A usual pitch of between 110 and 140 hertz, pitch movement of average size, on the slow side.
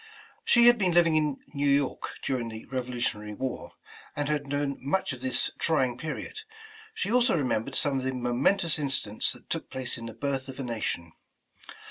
No: low, 135 Hz; average, 3.8 semitones; fast, 205 wpm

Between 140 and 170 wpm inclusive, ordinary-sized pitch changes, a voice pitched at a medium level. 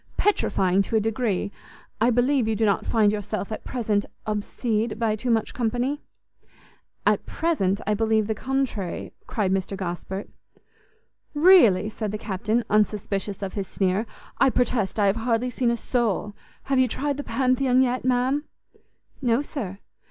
No: average, 155 wpm; average, 3.6 semitones; high, 220 Hz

